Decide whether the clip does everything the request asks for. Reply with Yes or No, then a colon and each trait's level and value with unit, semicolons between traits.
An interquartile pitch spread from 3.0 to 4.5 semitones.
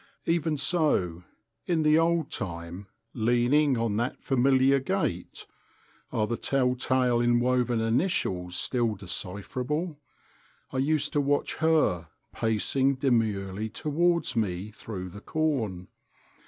No: wide, 5.6 semitones